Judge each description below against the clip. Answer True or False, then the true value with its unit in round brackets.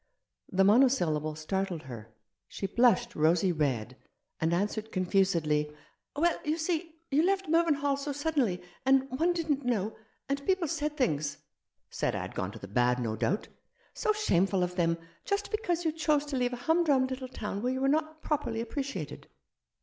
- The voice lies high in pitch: True (250 Hz)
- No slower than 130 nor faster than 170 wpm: False (190 wpm)